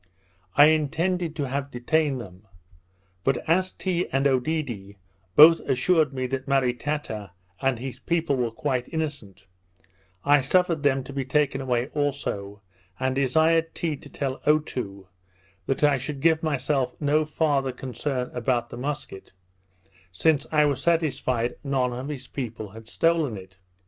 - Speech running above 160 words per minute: No, average, 145 wpm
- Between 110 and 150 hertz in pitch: Yes, low, 135 Hz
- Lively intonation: No, average, 3.5 semitones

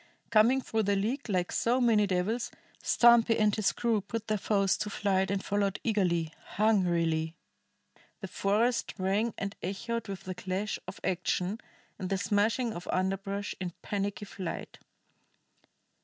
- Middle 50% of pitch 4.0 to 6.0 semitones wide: No, average, 2.9 semitones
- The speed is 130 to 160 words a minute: Yes, average, 145 wpm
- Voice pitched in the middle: No, high, 200 Hz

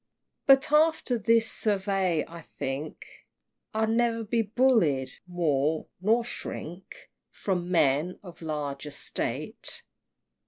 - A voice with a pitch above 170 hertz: Yes, medium, 185 Hz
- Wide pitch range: Yes, wide, 6.8 semitones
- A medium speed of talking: No, slow, 105 wpm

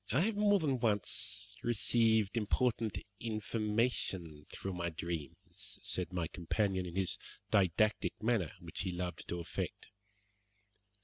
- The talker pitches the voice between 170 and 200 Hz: No, low, 100 Hz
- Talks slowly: Yes, slow, 125 wpm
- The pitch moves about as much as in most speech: Yes, average, 4.6 semitones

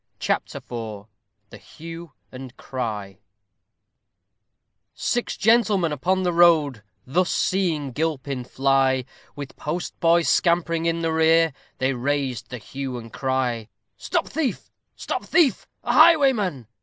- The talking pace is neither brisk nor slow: No, slow, 120 wpm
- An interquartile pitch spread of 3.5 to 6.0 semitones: Yes, average, 5.1 semitones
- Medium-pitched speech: Yes, medium, 150 Hz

